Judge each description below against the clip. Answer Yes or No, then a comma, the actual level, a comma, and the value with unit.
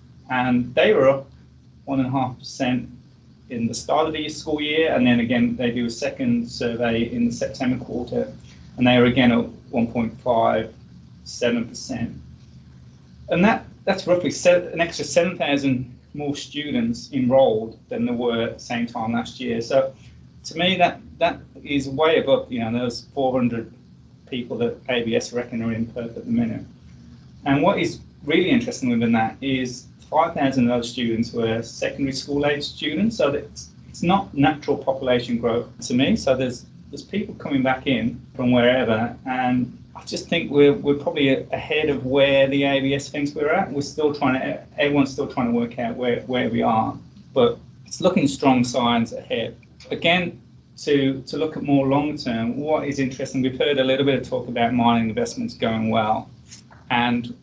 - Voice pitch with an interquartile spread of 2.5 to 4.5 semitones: Yes, average, 3.2 semitones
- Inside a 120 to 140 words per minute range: No, average, 180 wpm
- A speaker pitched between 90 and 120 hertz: No, low, 130 Hz